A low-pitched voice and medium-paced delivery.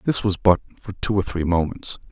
No: very low, 95 Hz; fast, 225 wpm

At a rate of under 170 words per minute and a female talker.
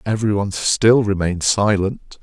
No: slow, 135 wpm; male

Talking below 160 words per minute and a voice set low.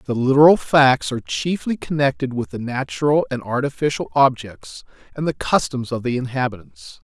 Yes: average, 150 wpm; low, 125 Hz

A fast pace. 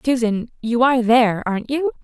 No: average, 175 wpm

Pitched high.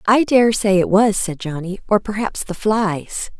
Yes: high, 205 Hz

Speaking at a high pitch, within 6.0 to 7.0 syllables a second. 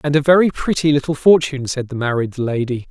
No: medium, 140 Hz; 6.1 syllables/s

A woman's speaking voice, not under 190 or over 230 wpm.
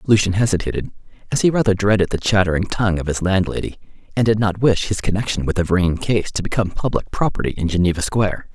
No: male; fast, 205 wpm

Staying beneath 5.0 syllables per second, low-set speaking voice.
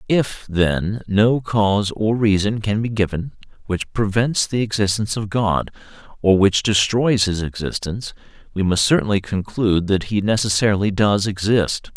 Yes: 4.7 syllables/s; low, 105 Hz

